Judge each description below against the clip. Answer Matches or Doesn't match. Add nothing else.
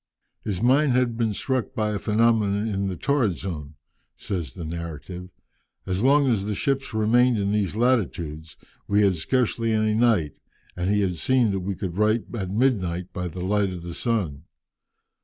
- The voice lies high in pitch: Doesn't match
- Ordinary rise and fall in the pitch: Matches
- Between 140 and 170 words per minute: Doesn't match